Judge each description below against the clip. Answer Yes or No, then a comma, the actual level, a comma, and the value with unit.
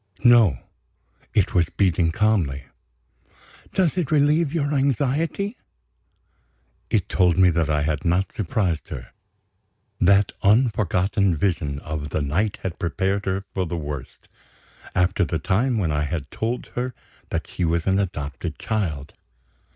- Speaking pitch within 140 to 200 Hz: No, very low, 95 Hz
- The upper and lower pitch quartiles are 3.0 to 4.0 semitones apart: No, wide, 5.4 semitones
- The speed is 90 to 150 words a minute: Yes, slow, 135 wpm